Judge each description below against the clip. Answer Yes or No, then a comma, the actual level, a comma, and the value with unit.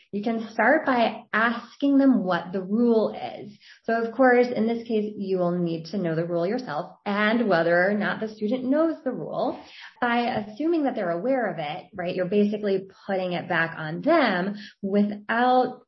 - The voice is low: No, high, 215 Hz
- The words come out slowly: No, average, 185 wpm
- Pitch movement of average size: Yes, average, 4.3 semitones